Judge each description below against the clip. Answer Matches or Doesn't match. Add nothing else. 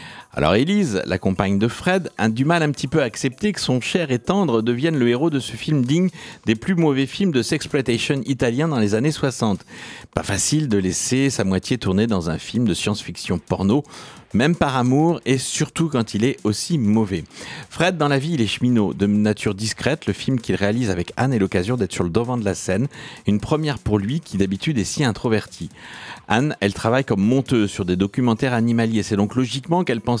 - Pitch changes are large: Matches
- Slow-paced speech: Doesn't match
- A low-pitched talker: Matches